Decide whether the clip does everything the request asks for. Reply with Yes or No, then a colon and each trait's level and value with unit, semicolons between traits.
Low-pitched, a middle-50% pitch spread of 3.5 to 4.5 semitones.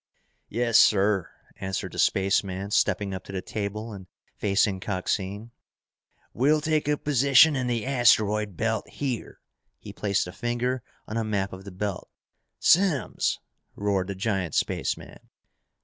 Yes: low, 105 Hz; average, 3.8 semitones